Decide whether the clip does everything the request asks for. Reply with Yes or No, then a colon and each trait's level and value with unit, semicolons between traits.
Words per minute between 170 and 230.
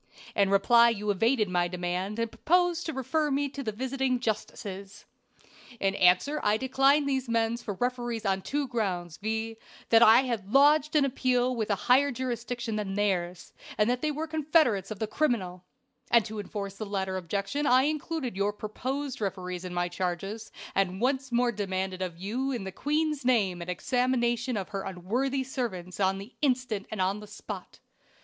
Yes: average, 180 wpm